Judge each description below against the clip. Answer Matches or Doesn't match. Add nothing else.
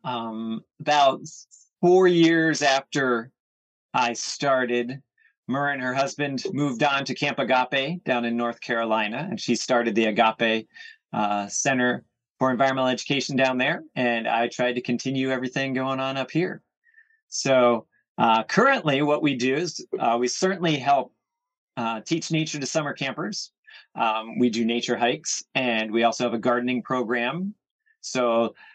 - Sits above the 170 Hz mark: Doesn't match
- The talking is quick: Doesn't match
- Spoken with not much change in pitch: Doesn't match